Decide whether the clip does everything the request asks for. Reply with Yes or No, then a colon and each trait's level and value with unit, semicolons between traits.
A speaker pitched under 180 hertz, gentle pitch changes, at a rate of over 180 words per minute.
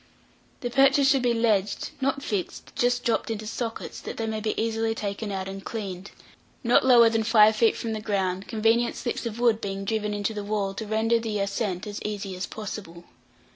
No: high, 220 Hz; narrow, 2.3 semitones; average, 200 wpm